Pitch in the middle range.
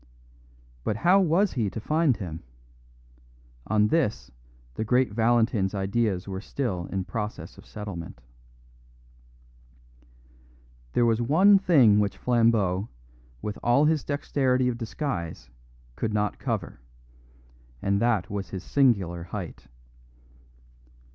No: low, 110 Hz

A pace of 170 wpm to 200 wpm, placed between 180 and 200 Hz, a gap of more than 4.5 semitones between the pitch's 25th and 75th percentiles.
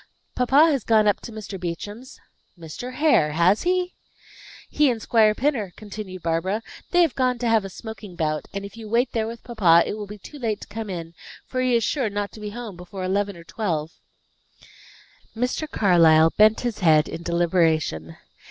No: average, 190 wpm; high, 210 Hz; average, 5.3 semitones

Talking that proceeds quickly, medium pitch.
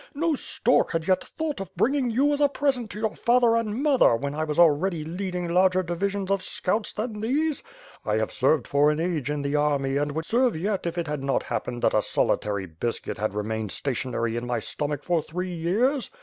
Yes: fast, 220 wpm; medium, 175 Hz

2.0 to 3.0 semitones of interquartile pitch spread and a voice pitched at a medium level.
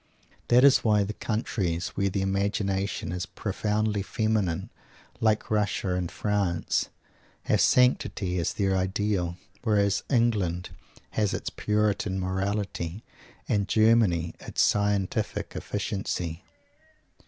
No: narrow, 2.4 semitones; low, 100 Hz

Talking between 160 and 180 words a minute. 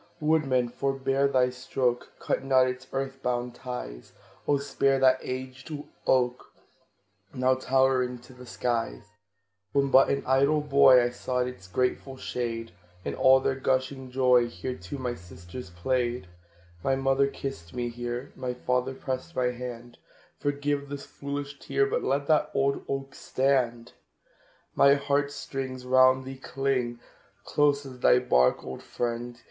No: average, 145 wpm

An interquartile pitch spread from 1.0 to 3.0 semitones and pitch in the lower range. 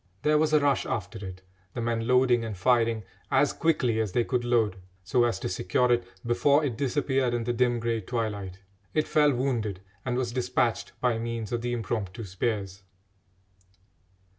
Yes: narrow, 2.5 semitones; low, 120 Hz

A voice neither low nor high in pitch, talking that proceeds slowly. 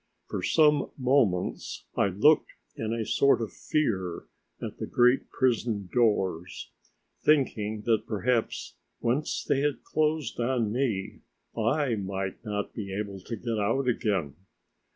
No: low, 115 Hz; slow, 130 wpm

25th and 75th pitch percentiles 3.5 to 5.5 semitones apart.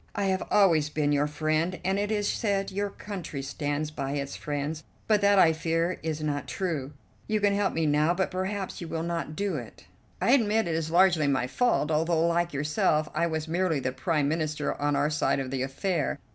Yes: average, 4.2 semitones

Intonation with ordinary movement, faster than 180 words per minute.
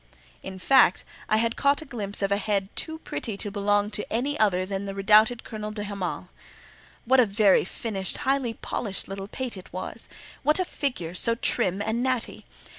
Yes: average, 3.7 semitones; average, 190 wpm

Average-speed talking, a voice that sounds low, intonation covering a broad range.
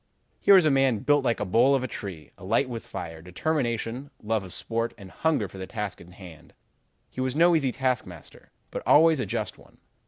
No: fast, 210 wpm; low, 115 Hz; wide, 6.1 semitones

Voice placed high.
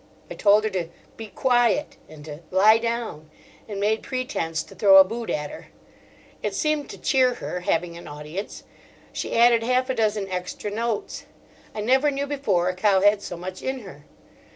Yes: high, 210 Hz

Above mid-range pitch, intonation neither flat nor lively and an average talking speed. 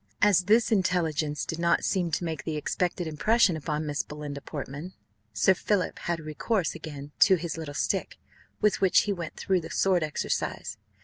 No: medium, 165 Hz; average, 3.7 semitones; average, 175 wpm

